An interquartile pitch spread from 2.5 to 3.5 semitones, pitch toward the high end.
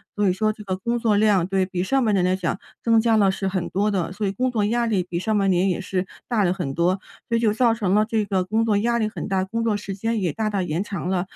Yes: average, 2.9 semitones; high, 205 Hz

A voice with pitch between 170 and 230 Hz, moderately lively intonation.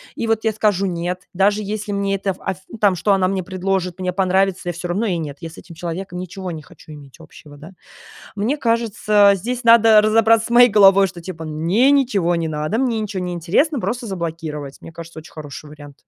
Yes: high, 190 Hz; average, 4.2 semitones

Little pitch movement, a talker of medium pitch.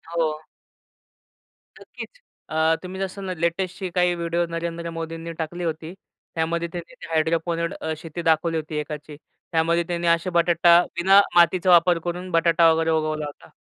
Yes: narrow, 1.2 semitones; medium, 170 Hz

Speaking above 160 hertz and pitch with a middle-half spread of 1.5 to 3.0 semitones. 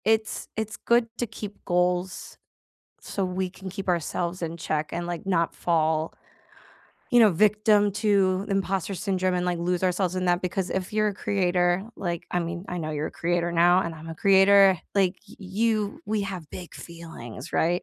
Yes: medium, 185 Hz; narrow, 2.5 semitones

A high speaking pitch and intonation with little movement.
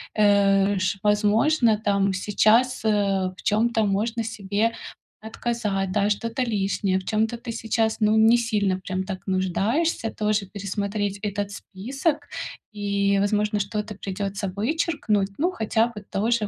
Yes: high, 210 Hz; narrow, 2.2 semitones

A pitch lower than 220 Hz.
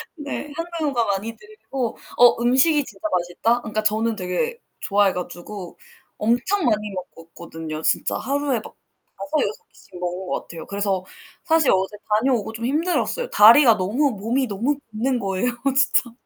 No: high, 230 Hz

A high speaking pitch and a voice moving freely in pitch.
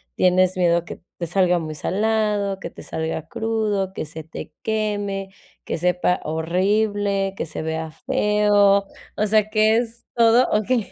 No: high, 195 Hz; average, 3.4 semitones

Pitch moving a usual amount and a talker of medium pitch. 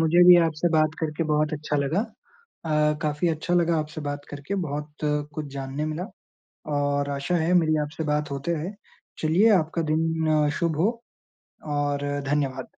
No: narrow, 1.9 semitones; medium, 155 Hz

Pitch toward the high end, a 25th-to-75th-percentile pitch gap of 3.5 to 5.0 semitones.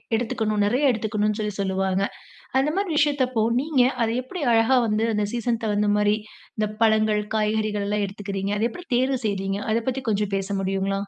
No: high, 215 Hz; average, 2.9 semitones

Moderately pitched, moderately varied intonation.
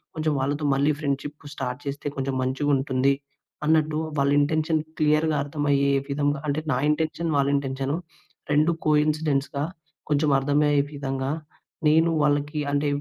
No: medium, 145 Hz; narrow, 1.6 semitones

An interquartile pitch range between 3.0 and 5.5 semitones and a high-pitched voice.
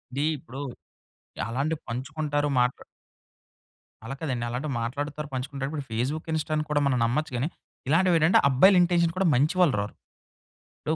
No: average, 3.6 semitones; medium, 145 Hz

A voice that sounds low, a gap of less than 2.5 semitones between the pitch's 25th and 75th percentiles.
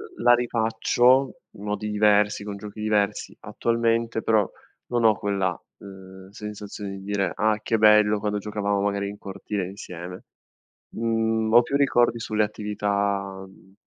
Yes: low, 105 Hz; narrow, 1.9 semitones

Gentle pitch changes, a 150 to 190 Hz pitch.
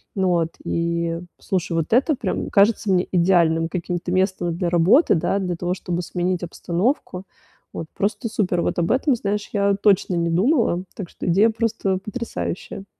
No: average, 3.2 semitones; medium, 185 Hz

